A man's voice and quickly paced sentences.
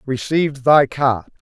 No: male; slow, 120 wpm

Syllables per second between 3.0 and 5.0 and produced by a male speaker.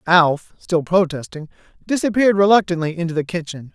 No: 5.6 syllables/s; male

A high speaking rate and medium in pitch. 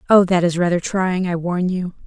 Yes: fast, 230 wpm; medium, 180 Hz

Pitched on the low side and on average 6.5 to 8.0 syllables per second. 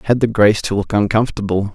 Yes: low, 105 Hz; 7.0 syllables/s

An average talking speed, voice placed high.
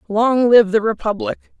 Yes: average, 150 wpm; high, 225 Hz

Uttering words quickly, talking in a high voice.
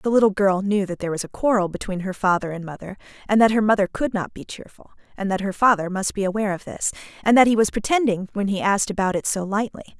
Yes: fast, 260 wpm; high, 200 Hz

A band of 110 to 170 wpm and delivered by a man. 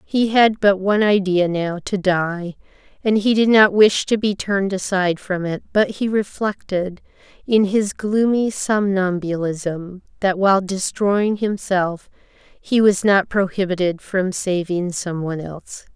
No: average, 145 wpm; female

